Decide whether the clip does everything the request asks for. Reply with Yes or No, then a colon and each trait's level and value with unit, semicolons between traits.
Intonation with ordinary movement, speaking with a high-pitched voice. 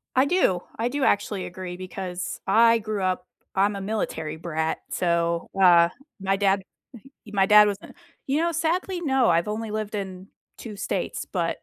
Yes: average, 3.6 semitones; high, 200 Hz